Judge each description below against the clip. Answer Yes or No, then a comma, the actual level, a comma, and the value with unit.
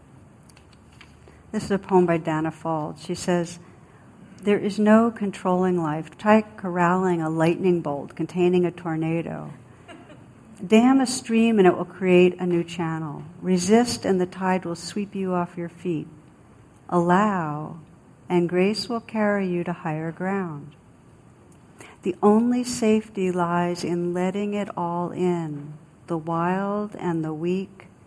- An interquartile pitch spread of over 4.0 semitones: No, average, 2.8 semitones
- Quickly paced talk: No, average, 140 wpm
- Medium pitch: Yes, medium, 180 Hz